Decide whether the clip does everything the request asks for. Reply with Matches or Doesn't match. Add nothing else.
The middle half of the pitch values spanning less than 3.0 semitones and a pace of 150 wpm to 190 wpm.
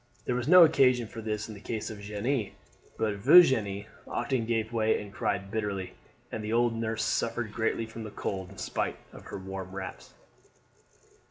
Matches